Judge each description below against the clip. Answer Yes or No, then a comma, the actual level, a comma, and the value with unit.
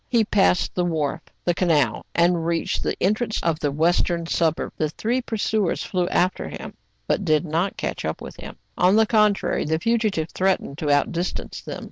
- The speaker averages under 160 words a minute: No, average, 185 wpm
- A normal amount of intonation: Yes, average, 4.1 semitones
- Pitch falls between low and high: Yes, medium, 175 Hz